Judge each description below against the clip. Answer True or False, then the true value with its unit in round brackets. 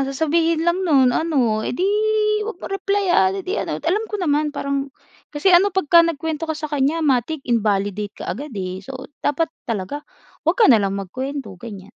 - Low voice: False (290 Hz)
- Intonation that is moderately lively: False (6.0 semitones)